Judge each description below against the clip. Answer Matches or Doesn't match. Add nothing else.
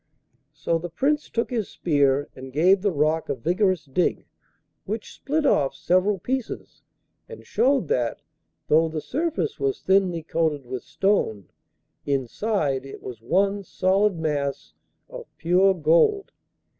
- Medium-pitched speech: Matches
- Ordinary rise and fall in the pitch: Doesn't match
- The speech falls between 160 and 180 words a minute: Doesn't match